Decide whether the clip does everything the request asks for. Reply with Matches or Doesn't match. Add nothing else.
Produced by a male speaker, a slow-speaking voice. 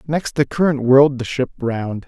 Doesn't match